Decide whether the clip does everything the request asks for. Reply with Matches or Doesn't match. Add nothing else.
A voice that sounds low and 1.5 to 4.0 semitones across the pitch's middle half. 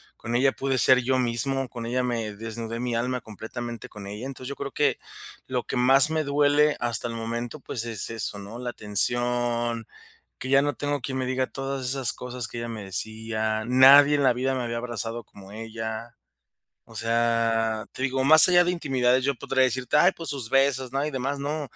Matches